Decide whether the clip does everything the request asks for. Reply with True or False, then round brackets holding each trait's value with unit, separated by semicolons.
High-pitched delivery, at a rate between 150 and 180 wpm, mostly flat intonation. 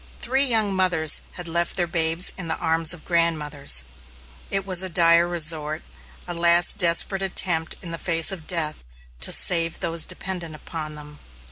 False (170 Hz; 160 wpm; 2.0 semitones)